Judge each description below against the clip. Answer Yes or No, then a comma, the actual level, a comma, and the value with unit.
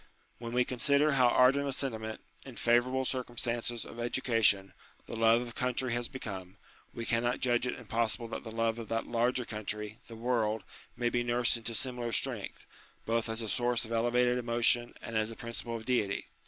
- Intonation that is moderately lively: No, narrow, 1.4 semitones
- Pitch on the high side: No, low, 120 Hz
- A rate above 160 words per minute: Yes, average, 185 wpm